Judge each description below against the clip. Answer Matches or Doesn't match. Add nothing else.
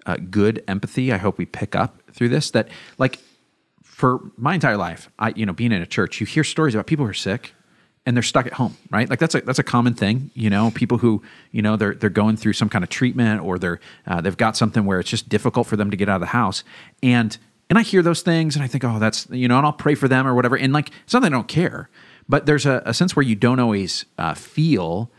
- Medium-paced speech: Doesn't match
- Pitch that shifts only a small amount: Doesn't match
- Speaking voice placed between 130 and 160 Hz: Doesn't match